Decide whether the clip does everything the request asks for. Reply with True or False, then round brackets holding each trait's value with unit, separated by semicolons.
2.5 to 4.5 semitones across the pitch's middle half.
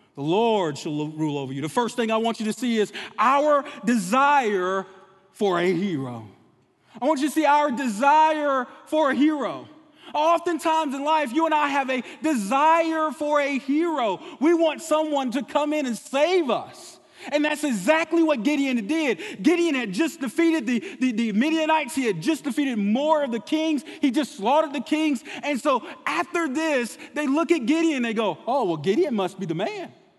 False (5.3 semitones)